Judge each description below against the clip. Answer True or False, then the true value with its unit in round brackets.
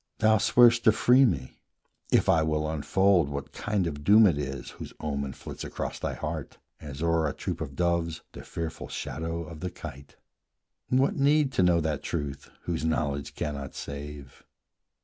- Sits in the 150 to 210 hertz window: False (80 Hz)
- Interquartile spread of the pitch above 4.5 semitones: True (5.1 semitones)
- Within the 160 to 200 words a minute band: True (170 wpm)